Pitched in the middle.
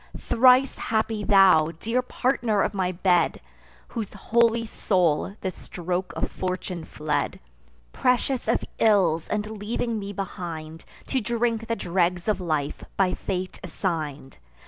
No: high, 195 Hz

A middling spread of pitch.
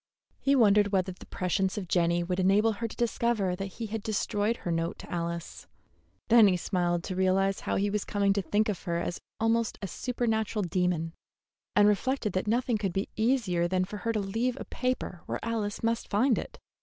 Yes: average, 3.5 semitones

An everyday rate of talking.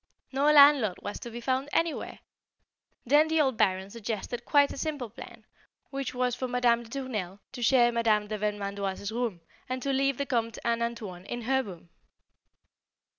Yes: average, 175 wpm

